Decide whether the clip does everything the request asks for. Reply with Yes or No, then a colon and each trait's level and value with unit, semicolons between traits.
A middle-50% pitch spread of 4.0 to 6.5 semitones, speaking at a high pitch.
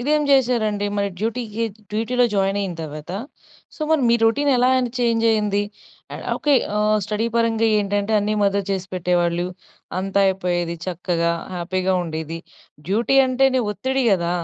Yes: average, 4.5 semitones; high, 205 Hz